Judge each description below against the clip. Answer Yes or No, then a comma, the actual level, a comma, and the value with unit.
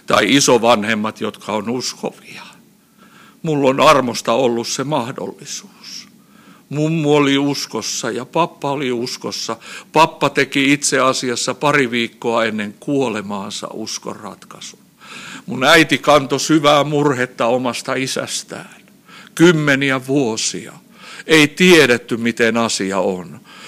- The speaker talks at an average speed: Yes, average, 105 wpm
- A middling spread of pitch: Yes, average, 3.6 semitones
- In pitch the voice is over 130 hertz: Yes, medium, 140 Hz